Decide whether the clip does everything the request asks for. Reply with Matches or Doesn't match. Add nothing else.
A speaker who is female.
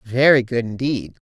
Matches